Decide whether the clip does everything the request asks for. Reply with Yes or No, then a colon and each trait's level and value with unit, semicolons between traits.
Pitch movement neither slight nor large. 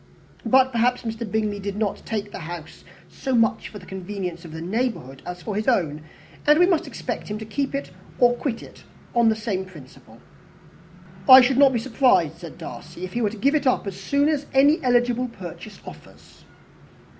Yes: average, 5.0 semitones